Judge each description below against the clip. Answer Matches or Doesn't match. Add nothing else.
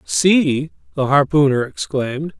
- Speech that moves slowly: Matches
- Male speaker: Matches